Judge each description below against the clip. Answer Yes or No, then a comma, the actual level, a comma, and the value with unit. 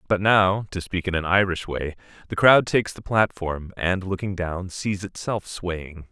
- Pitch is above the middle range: No, very low, 95 Hz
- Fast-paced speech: No, average, 185 wpm